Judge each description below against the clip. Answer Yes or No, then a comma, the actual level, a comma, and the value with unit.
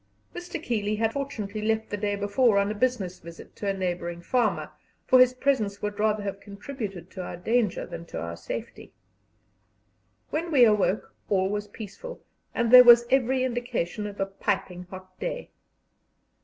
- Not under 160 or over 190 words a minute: Yes, average, 170 wpm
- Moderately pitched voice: No, high, 210 Hz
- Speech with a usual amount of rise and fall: Yes, average, 4.0 semitones